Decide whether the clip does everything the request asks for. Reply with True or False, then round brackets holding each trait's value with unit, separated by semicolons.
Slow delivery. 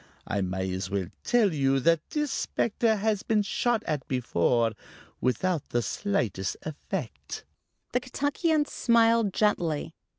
True (130 wpm)